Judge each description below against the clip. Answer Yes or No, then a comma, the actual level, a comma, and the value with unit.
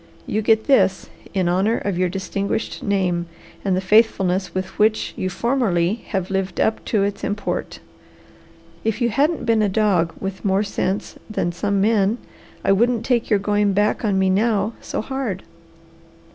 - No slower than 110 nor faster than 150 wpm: No, average, 165 wpm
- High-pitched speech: Yes, high, 200 Hz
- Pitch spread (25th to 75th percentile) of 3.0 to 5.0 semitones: No, narrow, 2.6 semitones